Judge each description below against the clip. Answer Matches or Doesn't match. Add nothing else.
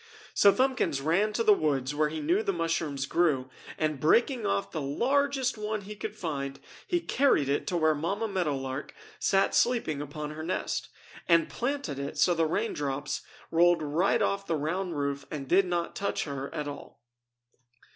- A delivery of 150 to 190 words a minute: Matches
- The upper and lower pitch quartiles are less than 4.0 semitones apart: Doesn't match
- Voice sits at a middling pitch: Matches